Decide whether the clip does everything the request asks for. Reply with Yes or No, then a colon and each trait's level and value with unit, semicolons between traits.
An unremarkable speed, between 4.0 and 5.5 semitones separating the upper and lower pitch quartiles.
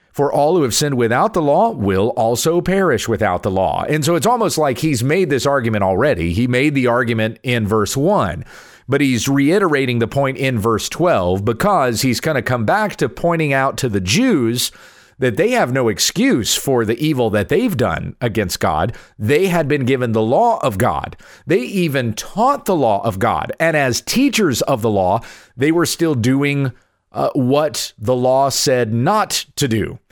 Yes: average, 195 wpm; average, 4.3 semitones